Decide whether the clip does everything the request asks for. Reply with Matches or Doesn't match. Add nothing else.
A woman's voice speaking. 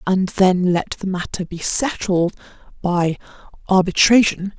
Matches